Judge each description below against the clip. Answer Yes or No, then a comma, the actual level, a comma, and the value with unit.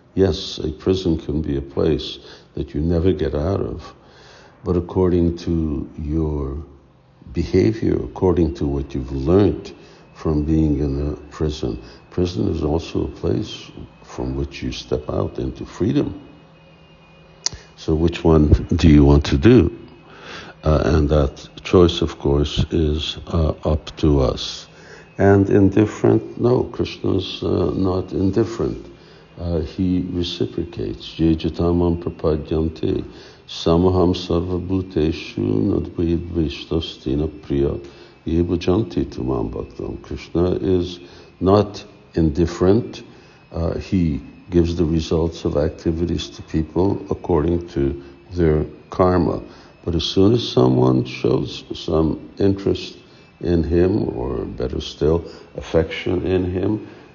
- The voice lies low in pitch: Yes, very low, 85 Hz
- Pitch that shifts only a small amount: No, average, 3.1 semitones